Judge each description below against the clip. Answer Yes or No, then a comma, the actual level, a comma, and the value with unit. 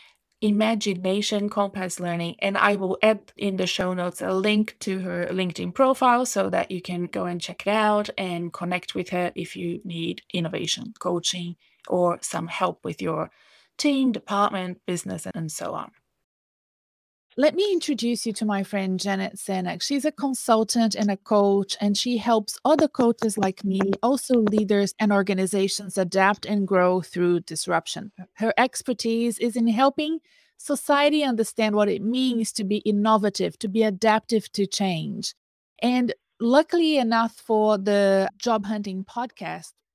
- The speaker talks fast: No, average, 155 wpm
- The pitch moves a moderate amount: Yes, average, 3.4 semitones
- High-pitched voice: Yes, high, 205 Hz